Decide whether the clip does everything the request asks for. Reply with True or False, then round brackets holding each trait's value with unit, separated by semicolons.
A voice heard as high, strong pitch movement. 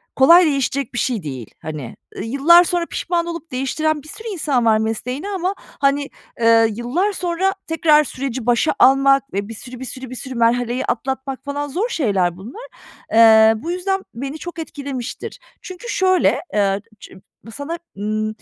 True (275 Hz; 6.6 semitones)